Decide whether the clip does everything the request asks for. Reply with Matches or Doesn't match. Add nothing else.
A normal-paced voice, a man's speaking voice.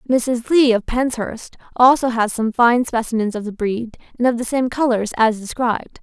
Doesn't match